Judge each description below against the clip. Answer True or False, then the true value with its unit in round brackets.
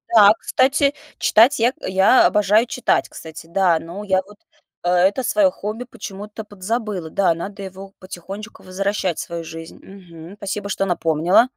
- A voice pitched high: True (195 Hz)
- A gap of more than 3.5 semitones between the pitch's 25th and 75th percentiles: False (3.2 semitones)